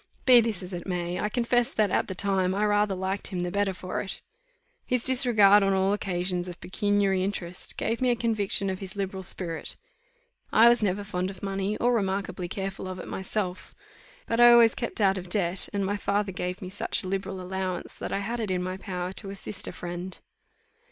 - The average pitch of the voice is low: No, high, 195 Hz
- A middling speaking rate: No, fast, 210 wpm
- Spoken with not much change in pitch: Yes, narrow, 2.1 semitones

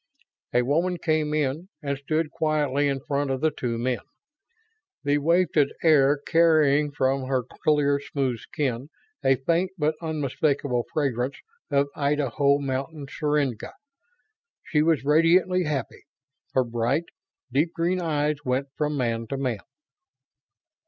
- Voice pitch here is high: No, medium, 145 Hz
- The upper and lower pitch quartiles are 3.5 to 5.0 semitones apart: No, average, 2.7 semitones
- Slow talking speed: Yes, slow, 130 wpm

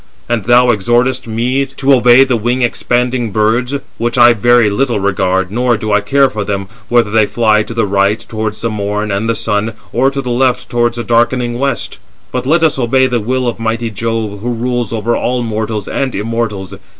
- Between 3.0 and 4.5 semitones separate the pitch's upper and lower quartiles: No, narrow, 2.5 semitones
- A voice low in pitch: Yes, low, 115 Hz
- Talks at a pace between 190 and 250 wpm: Yes, average, 200 wpm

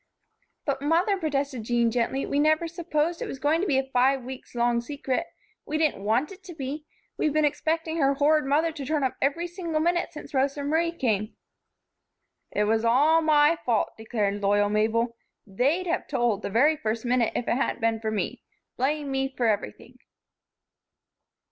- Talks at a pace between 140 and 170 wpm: No, average, 180 wpm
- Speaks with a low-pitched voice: No, very high, 275 Hz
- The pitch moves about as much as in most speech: Yes, average, 4.8 semitones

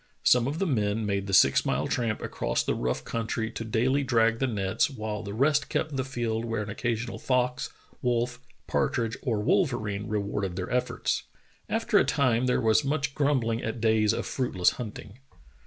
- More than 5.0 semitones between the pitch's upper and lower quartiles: No, average, 3.1 semitones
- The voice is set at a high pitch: No, low, 115 Hz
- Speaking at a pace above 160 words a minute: Yes, average, 180 wpm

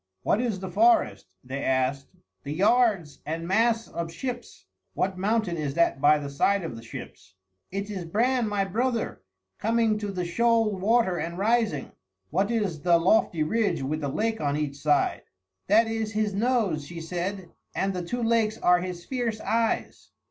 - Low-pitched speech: No, high, 195 Hz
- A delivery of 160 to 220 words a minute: Yes, average, 175 wpm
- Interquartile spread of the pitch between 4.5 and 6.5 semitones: Yes, wide, 5.5 semitones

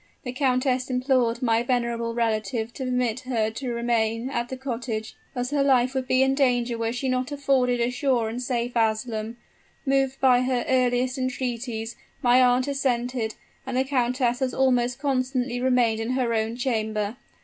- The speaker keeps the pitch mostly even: Yes, narrow, 1.7 semitones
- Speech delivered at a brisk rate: No, average, 170 wpm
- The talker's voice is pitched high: Yes, very high, 250 Hz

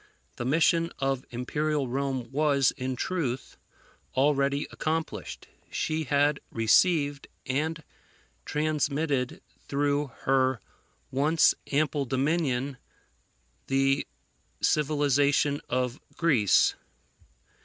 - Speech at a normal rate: No, slow, 80 wpm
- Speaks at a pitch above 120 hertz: Yes, medium, 140 Hz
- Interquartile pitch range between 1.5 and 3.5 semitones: Yes, narrow, 2.5 semitones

